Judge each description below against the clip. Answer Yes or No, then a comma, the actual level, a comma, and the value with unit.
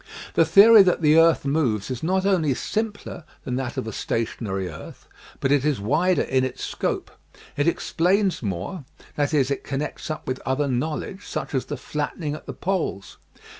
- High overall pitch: No, medium, 150 Hz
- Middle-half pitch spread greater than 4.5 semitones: Yes, average, 5.2 semitones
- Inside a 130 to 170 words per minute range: No, average, 180 wpm